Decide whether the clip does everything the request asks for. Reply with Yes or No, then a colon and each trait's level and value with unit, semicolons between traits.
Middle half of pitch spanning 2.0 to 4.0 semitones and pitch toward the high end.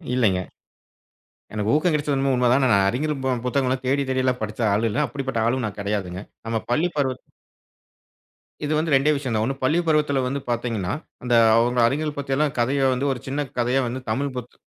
No: average, 3.3 semitones; low, 130 Hz